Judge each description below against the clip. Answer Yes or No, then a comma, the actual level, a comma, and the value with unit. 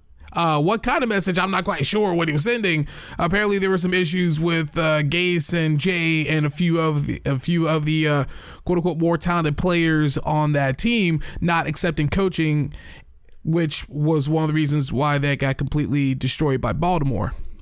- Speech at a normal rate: Yes, average, 195 wpm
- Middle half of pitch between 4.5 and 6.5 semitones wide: No, average, 3.1 semitones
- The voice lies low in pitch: No, medium, 155 Hz